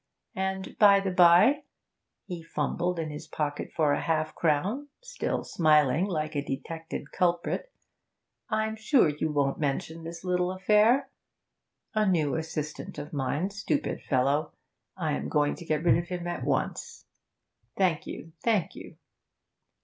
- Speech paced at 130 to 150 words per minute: Yes, average, 145 wpm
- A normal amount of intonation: Yes, average, 4.2 semitones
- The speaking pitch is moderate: Yes, medium, 165 Hz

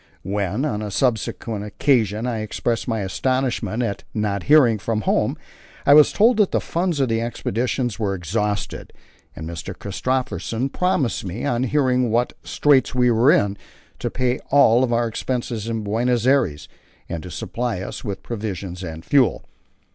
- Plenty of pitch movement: No, average, 3.9 semitones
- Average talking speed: Yes, average, 160 wpm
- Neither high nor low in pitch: No, low, 115 Hz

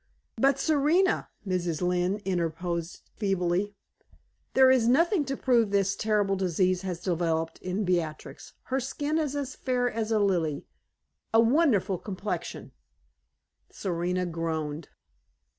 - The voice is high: Yes, high, 195 Hz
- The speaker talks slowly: Yes, slow, 125 wpm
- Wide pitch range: Yes, wide, 6.1 semitones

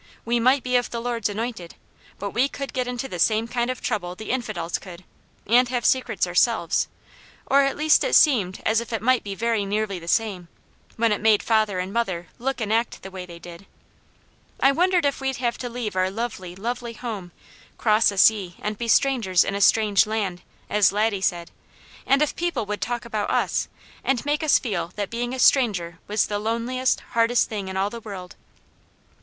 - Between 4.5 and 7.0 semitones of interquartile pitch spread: No, average, 3.8 semitones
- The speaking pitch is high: Yes, high, 220 Hz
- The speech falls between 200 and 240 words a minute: Yes, fast, 205 wpm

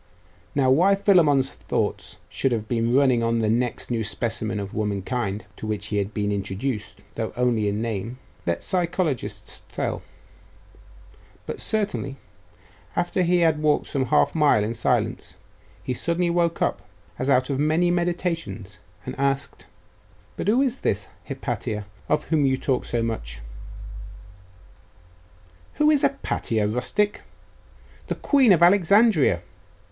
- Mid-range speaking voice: No, low, 130 Hz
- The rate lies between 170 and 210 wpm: No, average, 140 wpm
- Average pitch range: No, wide, 7.9 semitones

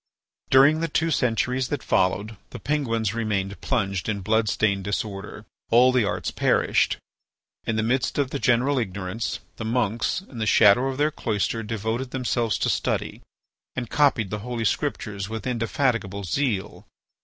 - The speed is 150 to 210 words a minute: Yes, average, 155 wpm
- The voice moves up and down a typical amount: Yes, average, 3.8 semitones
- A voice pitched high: No, low, 115 Hz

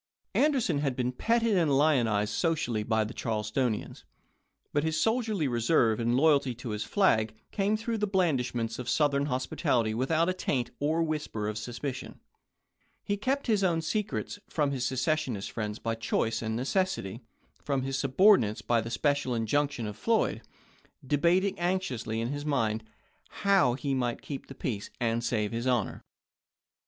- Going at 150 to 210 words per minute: Yes, average, 160 wpm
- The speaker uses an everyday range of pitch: No, wide, 6.2 semitones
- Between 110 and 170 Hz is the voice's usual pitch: Yes, low, 135 Hz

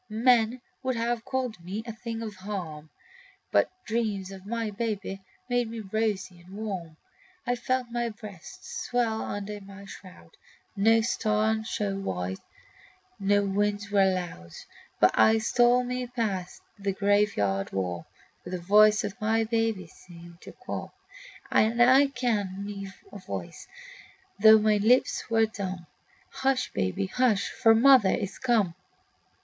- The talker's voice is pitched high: Yes, high, 210 Hz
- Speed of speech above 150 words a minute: No, average, 145 wpm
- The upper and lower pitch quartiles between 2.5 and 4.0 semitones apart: Yes, average, 3.0 semitones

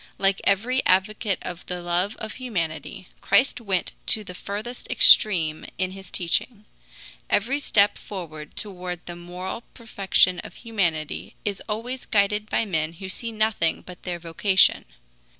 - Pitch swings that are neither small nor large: Yes, average, 3.4 semitones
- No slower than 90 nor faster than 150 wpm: Yes, average, 145 wpm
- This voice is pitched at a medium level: No, high, 195 Hz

